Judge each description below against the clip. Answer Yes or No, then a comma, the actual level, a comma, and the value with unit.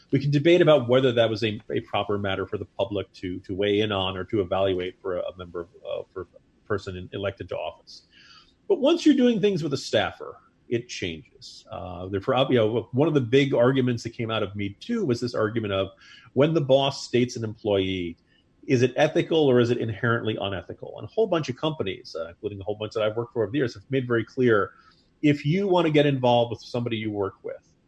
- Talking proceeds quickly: Yes, fast, 235 wpm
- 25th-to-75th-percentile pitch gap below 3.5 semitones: No, wide, 5.6 semitones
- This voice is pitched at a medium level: No, low, 115 Hz